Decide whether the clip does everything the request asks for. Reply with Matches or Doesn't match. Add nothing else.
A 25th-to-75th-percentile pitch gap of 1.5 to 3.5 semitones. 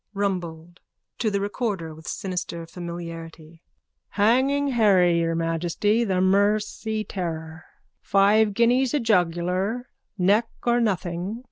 Doesn't match